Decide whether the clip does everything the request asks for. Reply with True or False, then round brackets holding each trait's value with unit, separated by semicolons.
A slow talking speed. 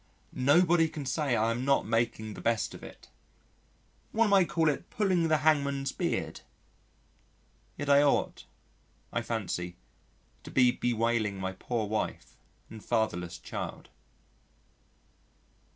True (125 wpm)